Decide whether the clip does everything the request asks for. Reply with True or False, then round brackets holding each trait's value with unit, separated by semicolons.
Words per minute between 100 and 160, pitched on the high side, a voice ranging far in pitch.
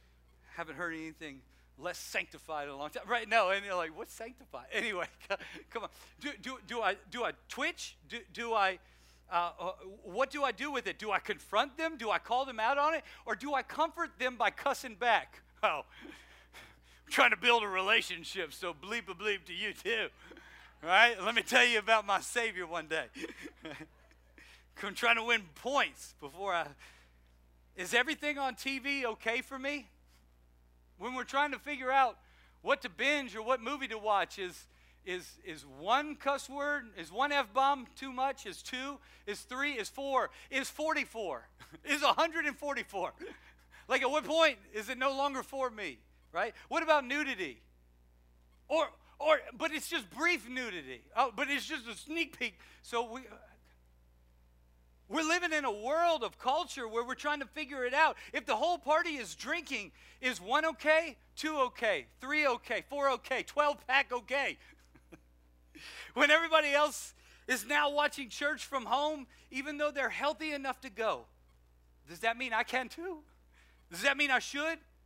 False (175 wpm; 255 Hz; 7.6 semitones)